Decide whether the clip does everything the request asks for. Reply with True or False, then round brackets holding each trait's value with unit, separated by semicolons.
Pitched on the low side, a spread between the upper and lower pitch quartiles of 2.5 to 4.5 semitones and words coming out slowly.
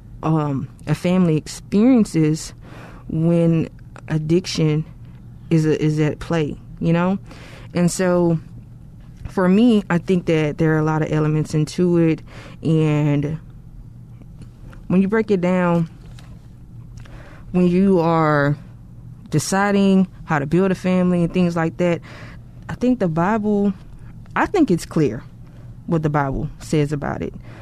False (155 Hz; 3.9 semitones; 130 wpm)